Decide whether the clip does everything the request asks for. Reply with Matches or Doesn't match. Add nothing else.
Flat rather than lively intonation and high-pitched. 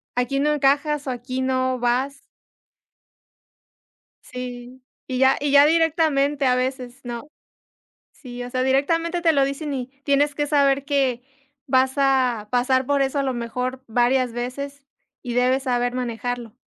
Matches